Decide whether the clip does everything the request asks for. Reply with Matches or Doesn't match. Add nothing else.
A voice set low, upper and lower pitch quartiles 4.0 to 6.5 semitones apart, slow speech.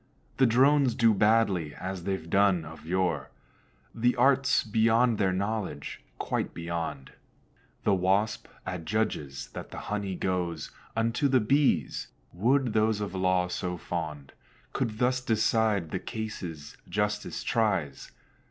Matches